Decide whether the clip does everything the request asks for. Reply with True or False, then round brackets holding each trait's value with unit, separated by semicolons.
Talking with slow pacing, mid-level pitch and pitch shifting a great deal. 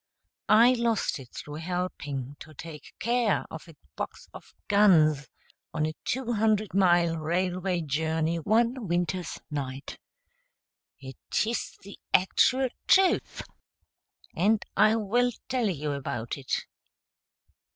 True (120 wpm; 180 Hz; 6.0 semitones)